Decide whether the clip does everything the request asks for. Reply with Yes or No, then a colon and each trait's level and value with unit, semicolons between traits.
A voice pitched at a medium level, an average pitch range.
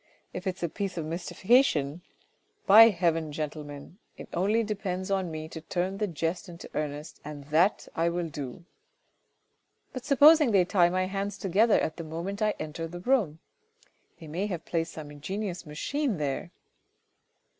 Yes: medium, 175 Hz; average, 4.1 semitones